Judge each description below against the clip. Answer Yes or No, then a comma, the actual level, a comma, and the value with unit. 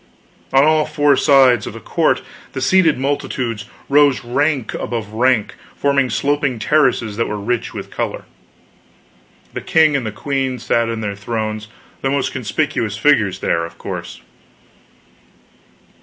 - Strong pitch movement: No, average, 4.4 semitones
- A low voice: Yes, low, 130 Hz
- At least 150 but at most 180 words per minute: No, average, 140 wpm